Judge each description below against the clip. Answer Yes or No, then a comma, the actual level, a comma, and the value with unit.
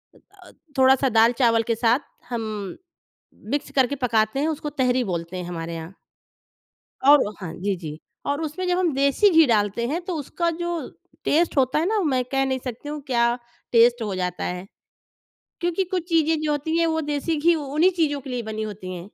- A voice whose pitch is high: Yes, very high, 265 Hz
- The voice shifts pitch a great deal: Yes, wide, 6.3 semitones